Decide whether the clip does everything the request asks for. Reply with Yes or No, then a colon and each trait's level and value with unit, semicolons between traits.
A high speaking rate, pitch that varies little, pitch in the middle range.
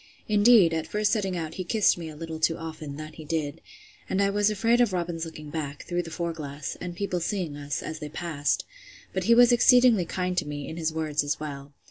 No: fast, 230 wpm; average, 4.2 semitones; medium, 165 Hz